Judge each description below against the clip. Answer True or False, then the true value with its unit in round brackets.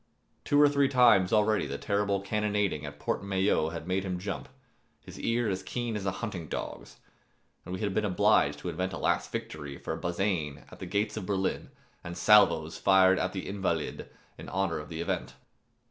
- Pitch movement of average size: True (3.4 semitones)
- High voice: False (95 Hz)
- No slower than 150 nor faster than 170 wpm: False (200 wpm)